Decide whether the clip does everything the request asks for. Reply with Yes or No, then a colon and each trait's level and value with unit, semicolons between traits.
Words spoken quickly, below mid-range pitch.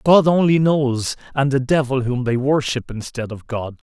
No: average, 185 wpm; low, 130 Hz